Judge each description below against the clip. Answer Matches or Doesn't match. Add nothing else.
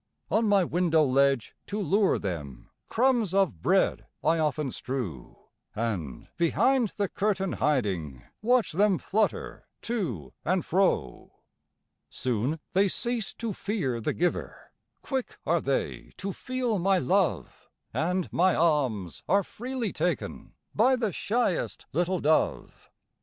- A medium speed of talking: Doesn't match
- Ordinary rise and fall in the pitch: Doesn't match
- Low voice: Doesn't match